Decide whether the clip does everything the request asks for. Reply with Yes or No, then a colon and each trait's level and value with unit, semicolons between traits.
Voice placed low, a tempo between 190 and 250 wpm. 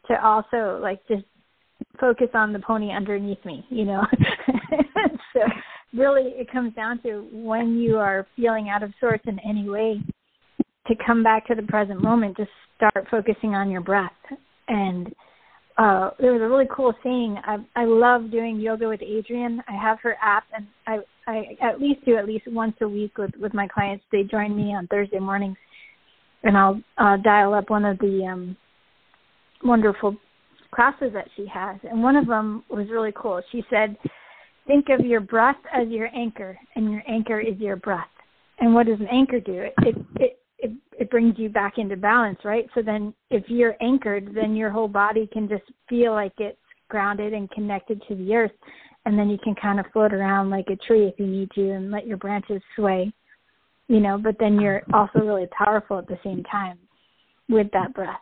No: high, 215 Hz; average, 195 wpm